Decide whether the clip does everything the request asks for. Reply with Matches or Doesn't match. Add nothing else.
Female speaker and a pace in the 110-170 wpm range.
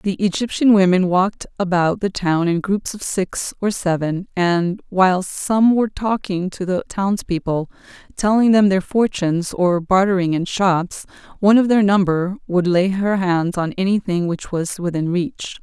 Matches